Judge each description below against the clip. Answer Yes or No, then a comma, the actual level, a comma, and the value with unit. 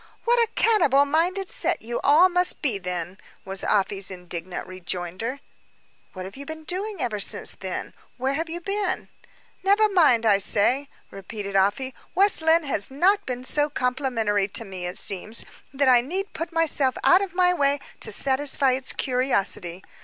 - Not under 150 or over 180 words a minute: Yes, average, 170 wpm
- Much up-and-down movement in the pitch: Yes, wide, 8.9 semitones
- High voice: Yes, very high, 265 Hz